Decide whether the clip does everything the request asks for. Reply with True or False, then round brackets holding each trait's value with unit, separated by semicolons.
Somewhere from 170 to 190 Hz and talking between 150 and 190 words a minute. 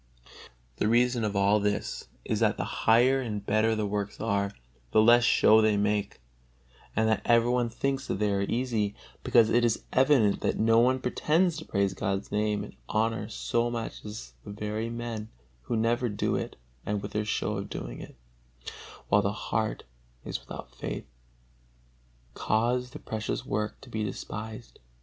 False (110 Hz; 170 wpm)